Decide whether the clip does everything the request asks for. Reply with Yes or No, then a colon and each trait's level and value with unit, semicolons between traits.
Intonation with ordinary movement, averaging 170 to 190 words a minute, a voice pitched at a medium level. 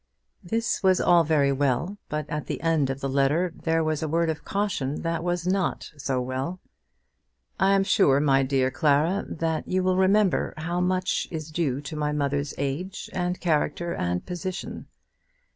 Yes: average, 4.3 semitones; average, 175 wpm; medium, 160 Hz